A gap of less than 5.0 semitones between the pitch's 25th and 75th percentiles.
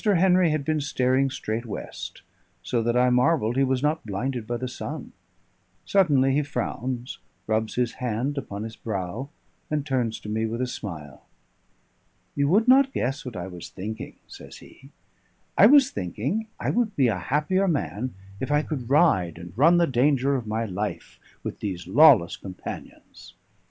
No: average, 5.3 semitones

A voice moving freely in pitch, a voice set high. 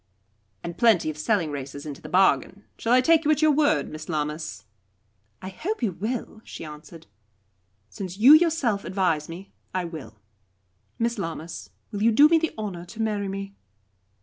Yes: wide, 7.0 semitones; high, 195 Hz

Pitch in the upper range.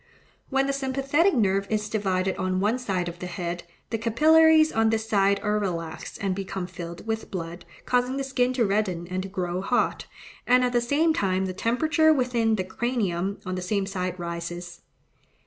Yes: high, 200 Hz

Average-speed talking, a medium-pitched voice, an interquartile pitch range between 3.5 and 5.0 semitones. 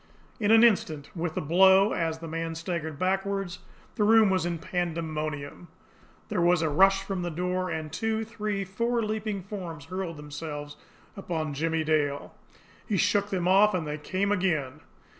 Yes: average, 165 wpm; medium, 180 Hz; average, 3.8 semitones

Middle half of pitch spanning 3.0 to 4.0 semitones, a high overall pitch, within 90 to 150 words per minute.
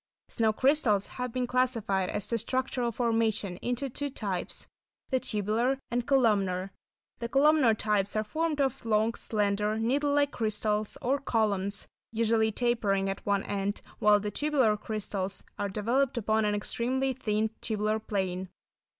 Yes: average, 3.3 semitones; high, 220 Hz; average, 145 wpm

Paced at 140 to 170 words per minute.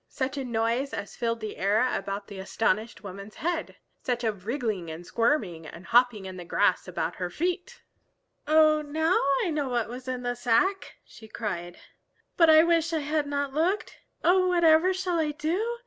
No: average, 180 wpm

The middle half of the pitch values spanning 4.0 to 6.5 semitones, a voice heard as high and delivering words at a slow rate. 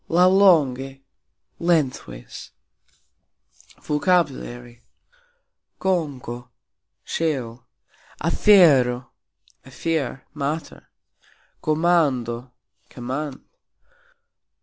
No: average, 5.1 semitones; medium, 140 Hz; slow, 40 wpm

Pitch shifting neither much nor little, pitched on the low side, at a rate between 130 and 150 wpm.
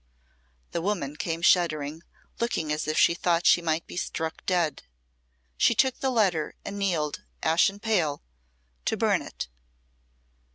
No: average, 4.1 semitones; medium, 170 Hz; average, 140 wpm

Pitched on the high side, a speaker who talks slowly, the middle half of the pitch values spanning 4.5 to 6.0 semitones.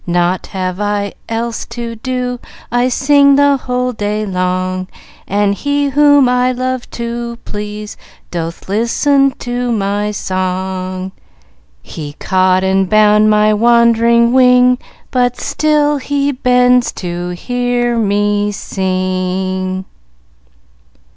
Yes: high, 220 Hz; slow, 115 wpm; average, 4.8 semitones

